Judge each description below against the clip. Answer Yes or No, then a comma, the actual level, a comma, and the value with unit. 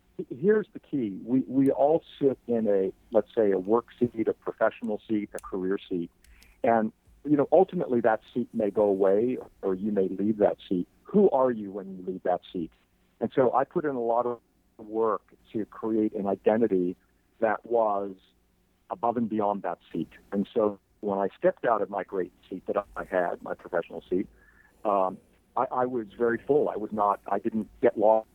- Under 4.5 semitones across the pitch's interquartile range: Yes, average, 3.6 semitones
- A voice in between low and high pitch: No, low, 110 Hz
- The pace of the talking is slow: No, average, 195 wpm